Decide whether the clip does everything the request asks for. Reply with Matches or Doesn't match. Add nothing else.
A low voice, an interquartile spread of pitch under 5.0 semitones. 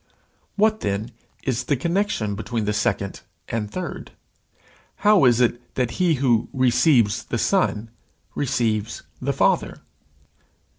Doesn't match